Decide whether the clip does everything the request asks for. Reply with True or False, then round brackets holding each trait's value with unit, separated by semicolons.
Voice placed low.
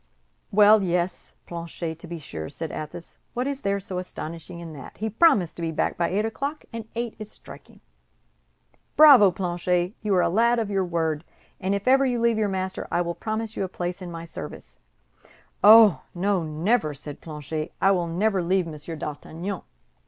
False (185 Hz)